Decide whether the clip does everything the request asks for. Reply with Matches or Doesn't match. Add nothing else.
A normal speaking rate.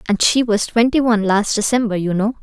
Doesn't match